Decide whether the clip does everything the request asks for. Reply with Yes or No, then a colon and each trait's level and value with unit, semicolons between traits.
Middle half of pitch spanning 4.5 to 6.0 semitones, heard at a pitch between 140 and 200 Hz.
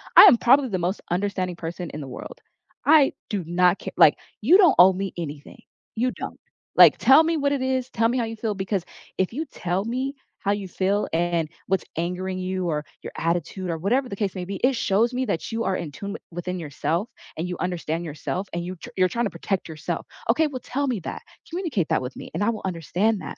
Yes: average, 5.3 semitones; high, 190 Hz